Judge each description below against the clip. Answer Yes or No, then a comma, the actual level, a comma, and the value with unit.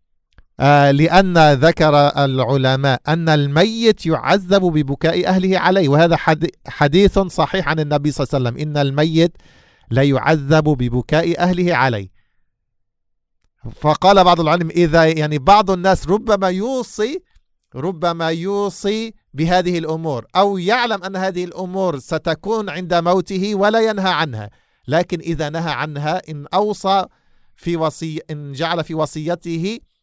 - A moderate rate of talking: No, slow, 125 wpm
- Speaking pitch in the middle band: Yes, medium, 165 Hz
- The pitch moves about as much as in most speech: Yes, average, 4.1 semitones